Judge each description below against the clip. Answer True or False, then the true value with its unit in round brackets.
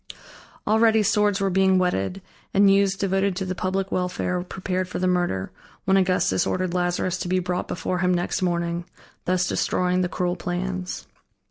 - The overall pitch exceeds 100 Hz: True (185 Hz)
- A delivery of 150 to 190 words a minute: True (165 wpm)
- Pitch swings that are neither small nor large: False (1.2 semitones)